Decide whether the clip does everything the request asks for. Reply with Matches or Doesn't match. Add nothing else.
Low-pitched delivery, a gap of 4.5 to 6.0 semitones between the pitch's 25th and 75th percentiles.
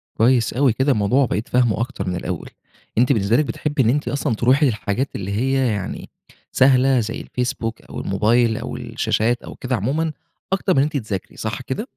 Doesn't match